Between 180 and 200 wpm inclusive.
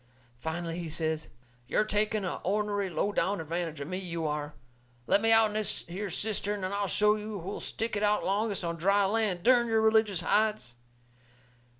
Yes: average, 185 wpm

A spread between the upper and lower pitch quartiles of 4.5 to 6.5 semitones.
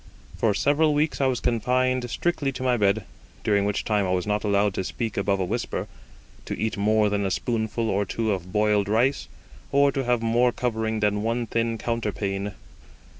No: average, 3.1 semitones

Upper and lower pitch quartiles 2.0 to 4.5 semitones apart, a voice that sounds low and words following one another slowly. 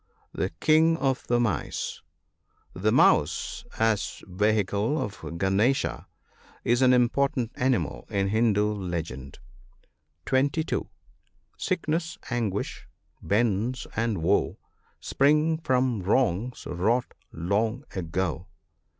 No: average, 5.1 semitones; low, 115 Hz; slow, 100 wpm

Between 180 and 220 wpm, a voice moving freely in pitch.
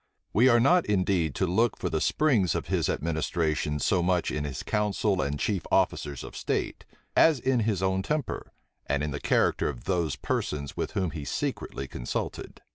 Yes: average, 185 wpm; wide, 6.0 semitones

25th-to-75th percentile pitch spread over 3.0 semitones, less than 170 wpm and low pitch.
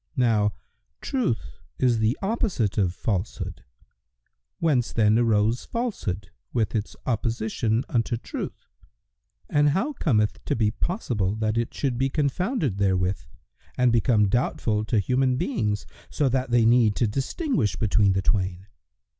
Yes: average, 3.8 semitones; average, 140 wpm; low, 115 Hz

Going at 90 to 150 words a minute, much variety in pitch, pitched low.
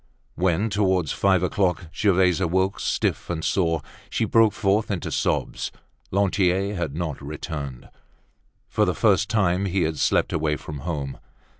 No: average, 145 wpm; average, 3.6 semitones; very low, 90 Hz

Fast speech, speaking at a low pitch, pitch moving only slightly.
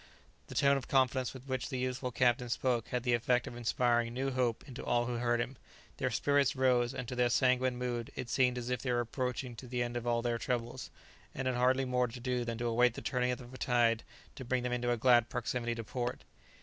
Yes: fast, 240 wpm; low, 125 Hz; narrow, 1.1 semitones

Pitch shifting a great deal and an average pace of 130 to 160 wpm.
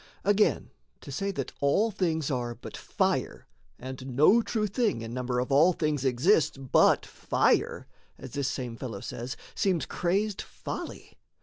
Yes: wide, 7.1 semitones; average, 150 wpm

